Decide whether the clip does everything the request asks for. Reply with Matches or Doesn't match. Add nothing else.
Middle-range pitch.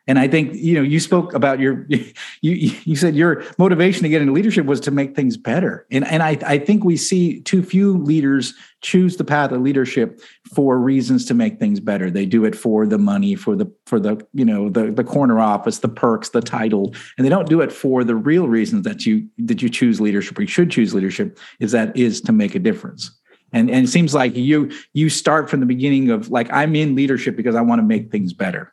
Matches